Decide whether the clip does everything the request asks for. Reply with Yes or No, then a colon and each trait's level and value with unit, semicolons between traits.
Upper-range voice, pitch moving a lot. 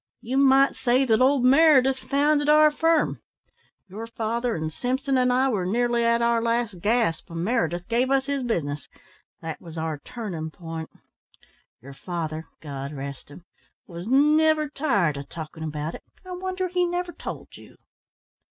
Yes: high, 235 Hz; wide, 8.7 semitones